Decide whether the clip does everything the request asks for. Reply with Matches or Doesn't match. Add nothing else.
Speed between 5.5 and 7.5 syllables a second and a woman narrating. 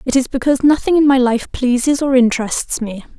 Matches